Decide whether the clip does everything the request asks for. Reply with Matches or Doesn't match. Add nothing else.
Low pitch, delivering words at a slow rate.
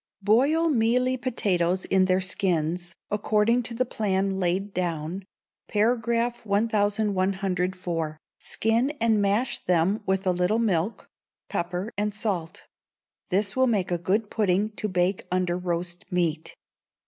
Doesn't match